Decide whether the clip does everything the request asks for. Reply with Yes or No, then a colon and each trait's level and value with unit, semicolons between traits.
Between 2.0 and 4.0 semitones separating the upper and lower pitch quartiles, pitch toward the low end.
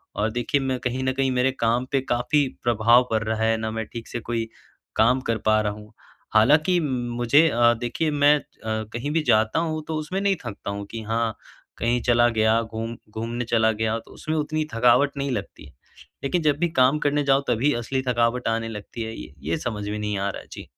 Yes: average, 3.7 semitones; low, 120 Hz